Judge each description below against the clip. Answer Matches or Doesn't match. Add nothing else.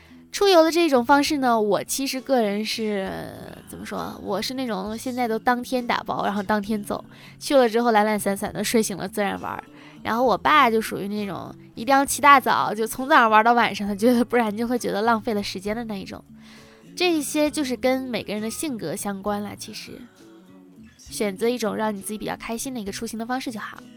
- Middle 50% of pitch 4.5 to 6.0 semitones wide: Doesn't match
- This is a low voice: Doesn't match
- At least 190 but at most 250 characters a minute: Doesn't match